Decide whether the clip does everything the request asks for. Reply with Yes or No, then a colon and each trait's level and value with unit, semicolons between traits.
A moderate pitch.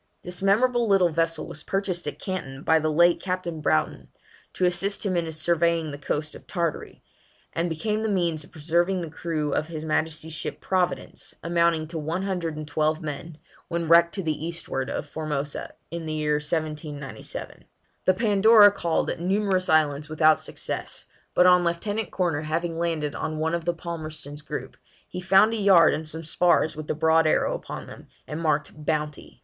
Yes: medium, 165 Hz